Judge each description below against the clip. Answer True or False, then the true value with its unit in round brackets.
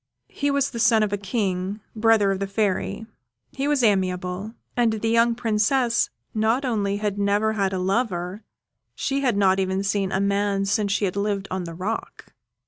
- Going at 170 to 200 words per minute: True (185 wpm)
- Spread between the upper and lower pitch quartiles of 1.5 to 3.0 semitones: True (2.6 semitones)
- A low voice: False (205 Hz)